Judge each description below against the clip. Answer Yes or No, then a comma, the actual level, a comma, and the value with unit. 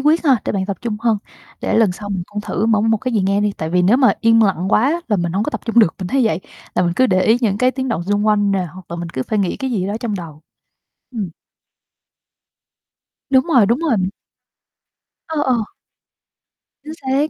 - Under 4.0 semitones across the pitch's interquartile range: No, average, 5.0 semitones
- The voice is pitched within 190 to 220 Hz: Yes, high, 210 Hz